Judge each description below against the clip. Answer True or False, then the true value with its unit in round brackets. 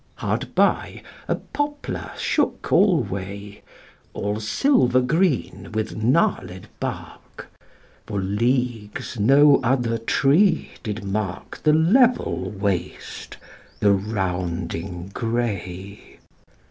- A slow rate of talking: True (90 wpm)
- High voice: False (110 Hz)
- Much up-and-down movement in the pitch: True (5.9 semitones)